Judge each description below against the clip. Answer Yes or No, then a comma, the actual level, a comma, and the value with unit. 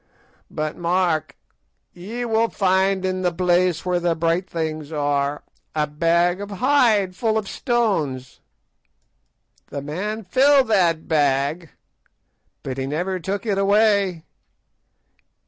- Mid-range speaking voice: Yes, medium, 180 Hz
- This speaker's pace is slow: Yes, slow, 120 wpm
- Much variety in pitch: No, average, 4.4 semitones